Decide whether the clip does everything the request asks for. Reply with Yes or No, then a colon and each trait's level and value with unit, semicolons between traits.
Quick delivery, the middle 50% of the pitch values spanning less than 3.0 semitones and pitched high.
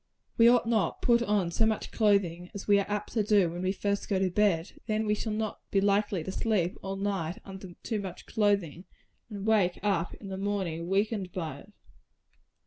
Yes: fast, 215 wpm; narrow, 2.4 semitones; high, 200 Hz